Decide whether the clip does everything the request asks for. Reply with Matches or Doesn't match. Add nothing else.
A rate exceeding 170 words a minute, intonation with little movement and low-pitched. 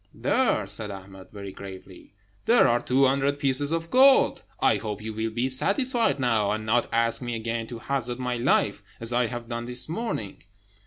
Doesn't match